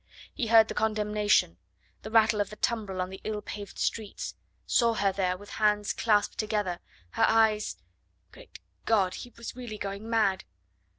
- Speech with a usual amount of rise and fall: No, narrow, 1.8 semitones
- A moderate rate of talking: Yes, average, 165 wpm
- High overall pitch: Yes, high, 210 Hz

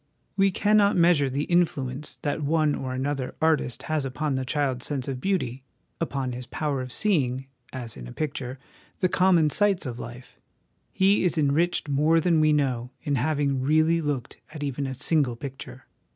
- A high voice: No, medium, 145 Hz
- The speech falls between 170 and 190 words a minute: Yes, average, 175 wpm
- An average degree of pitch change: Yes, average, 3.8 semitones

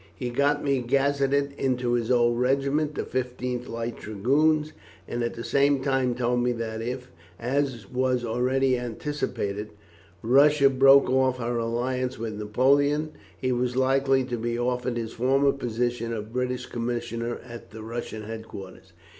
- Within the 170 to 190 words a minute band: No, average, 150 wpm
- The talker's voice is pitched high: No, low, 125 Hz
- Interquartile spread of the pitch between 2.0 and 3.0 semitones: Yes, narrow, 2.4 semitones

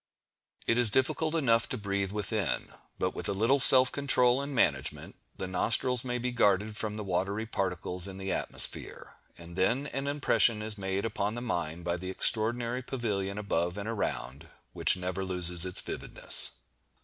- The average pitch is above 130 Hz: No, low, 105 Hz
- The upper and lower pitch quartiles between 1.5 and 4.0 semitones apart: No, average, 4.7 semitones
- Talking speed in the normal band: Yes, average, 170 wpm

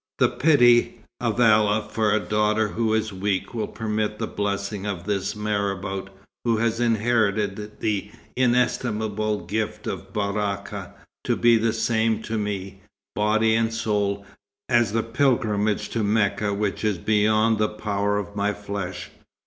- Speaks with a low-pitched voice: Yes, low, 105 Hz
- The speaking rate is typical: Yes, average, 145 wpm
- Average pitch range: No, narrow, 1.7 semitones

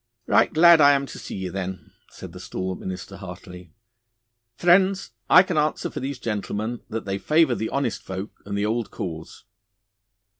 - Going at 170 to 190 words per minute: Yes, average, 175 wpm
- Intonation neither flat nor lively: No, wide, 7.2 semitones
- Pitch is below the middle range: Yes, low, 110 Hz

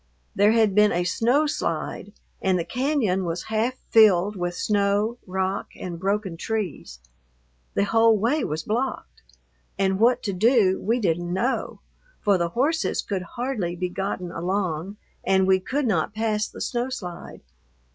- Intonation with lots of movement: No, average, 3.9 semitones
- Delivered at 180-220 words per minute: No, average, 155 wpm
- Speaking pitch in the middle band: No, high, 200 Hz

